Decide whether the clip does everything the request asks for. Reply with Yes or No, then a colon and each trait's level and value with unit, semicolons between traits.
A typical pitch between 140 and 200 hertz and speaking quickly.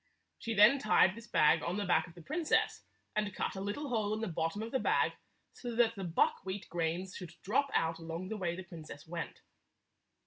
Yes: high, 190 Hz; fast, 210 wpm